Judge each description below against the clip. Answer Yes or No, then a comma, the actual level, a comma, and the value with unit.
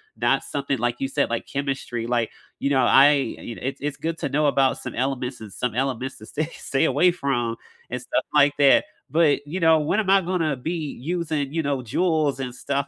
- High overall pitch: No, medium, 140 Hz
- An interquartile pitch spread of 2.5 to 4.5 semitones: Yes, average, 3.5 semitones